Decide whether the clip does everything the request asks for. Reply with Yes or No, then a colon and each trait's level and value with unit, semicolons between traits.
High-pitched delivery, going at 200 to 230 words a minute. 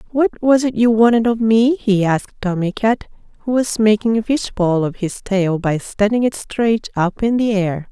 Yes: high, 215 Hz; fast, 205 wpm